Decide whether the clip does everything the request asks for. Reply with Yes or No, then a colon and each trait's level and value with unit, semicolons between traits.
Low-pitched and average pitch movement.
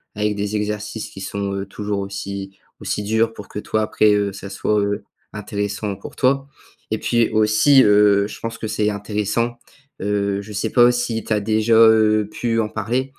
No: low, 105 Hz; narrow, 1.7 semitones